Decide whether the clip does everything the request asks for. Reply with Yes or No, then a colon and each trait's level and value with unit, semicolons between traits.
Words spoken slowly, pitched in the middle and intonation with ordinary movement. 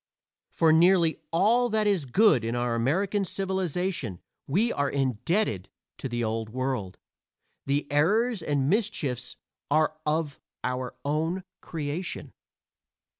No: slow, 120 wpm; medium, 155 Hz; wide, 6.9 semitones